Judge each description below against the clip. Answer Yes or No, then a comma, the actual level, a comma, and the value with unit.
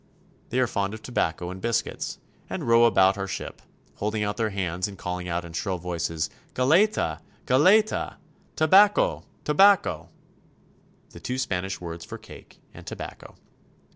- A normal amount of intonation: No, wide, 6.1 semitones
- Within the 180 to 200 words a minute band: No, average, 160 wpm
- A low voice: Yes, low, 100 Hz